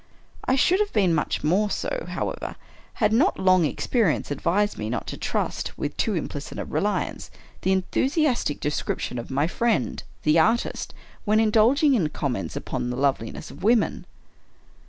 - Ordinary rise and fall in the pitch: No, wide, 7.9 semitones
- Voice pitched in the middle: No, high, 200 Hz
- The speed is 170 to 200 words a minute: No, average, 160 wpm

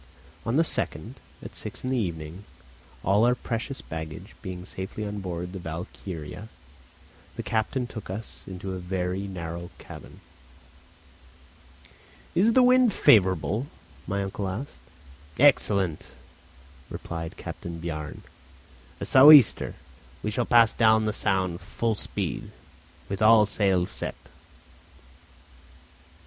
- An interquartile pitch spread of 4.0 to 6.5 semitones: Yes, average, 4.3 semitones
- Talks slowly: Yes, slow, 120 wpm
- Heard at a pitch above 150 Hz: No, low, 100 Hz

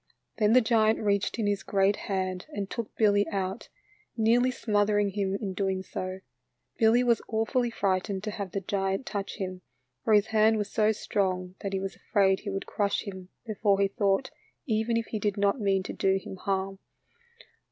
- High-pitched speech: Yes, high, 200 Hz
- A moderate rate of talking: Yes, average, 185 wpm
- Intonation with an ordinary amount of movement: No, narrow, 2.1 semitones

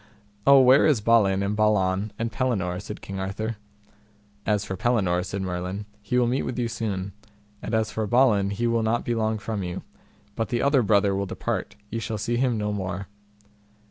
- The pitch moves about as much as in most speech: Yes, average, 3.1 semitones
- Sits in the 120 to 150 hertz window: No, low, 105 Hz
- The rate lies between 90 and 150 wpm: No, average, 195 wpm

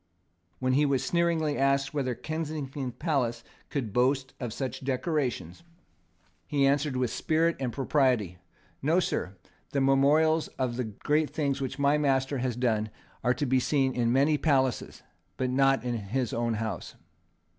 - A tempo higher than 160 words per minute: No, average, 155 wpm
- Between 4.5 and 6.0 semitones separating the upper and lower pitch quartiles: No, average, 2.9 semitones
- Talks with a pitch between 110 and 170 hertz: Yes, low, 135 Hz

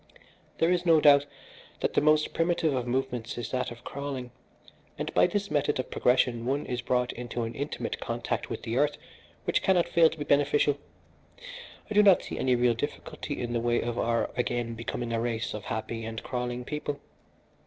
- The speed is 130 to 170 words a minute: No, average, 195 wpm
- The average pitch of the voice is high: No, low, 125 Hz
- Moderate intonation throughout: Yes, average, 3.7 semitones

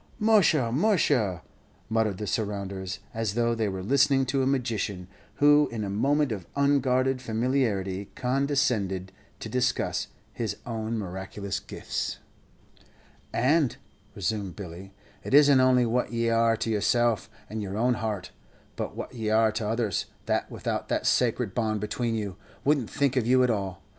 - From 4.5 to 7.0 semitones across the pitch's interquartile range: No, average, 4.1 semitones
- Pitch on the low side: Yes, low, 115 Hz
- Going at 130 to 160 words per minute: Yes, average, 155 wpm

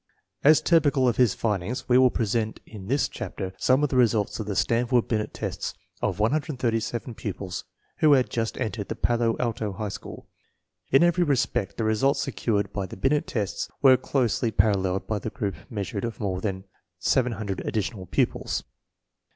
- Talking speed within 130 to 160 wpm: No, average, 180 wpm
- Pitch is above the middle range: No, low, 115 Hz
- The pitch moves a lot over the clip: No, average, 4.0 semitones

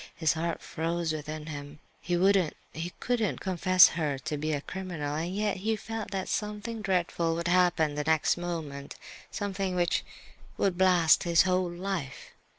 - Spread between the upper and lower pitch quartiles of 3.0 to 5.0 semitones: Yes, average, 3.3 semitones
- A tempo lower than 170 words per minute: Yes, average, 160 wpm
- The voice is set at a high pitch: No, medium, 175 Hz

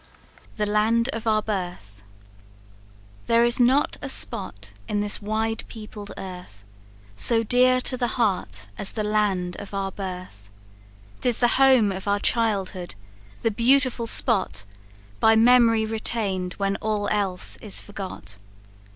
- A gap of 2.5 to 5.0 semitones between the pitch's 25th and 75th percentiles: Yes, average, 3.4 semitones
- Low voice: No, high, 210 Hz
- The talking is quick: No, slow, 135 wpm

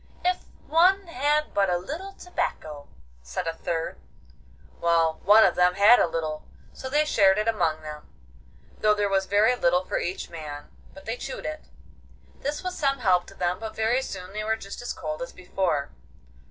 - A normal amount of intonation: No, wide, 6.8 semitones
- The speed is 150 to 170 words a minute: No, average, 185 wpm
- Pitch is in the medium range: No, high, 195 Hz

